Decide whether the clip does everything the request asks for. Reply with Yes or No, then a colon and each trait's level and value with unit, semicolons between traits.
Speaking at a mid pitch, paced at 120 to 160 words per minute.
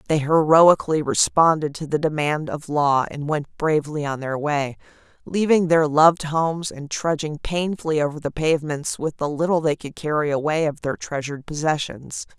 No: medium, 150 Hz; average, 170 wpm